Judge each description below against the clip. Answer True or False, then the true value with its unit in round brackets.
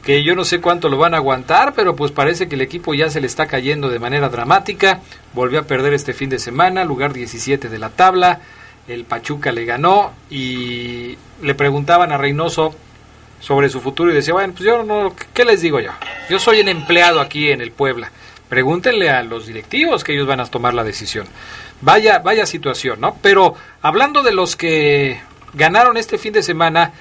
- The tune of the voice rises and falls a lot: True (6.1 semitones)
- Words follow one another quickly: True (200 wpm)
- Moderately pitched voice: True (145 Hz)